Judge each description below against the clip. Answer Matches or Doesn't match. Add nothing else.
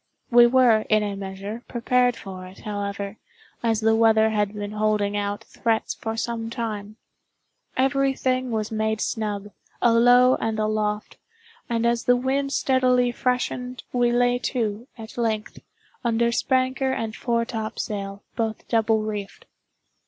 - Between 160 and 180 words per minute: Doesn't match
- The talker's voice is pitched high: Matches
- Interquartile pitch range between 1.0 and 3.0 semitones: Matches